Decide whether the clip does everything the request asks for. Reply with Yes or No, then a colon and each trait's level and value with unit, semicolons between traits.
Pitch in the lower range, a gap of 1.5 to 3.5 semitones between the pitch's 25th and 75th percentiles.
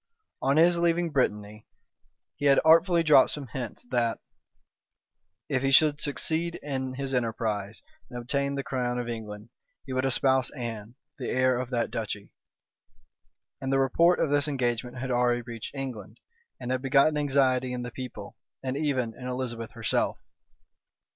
Yes: low, 130 Hz; narrow, 2.6 semitones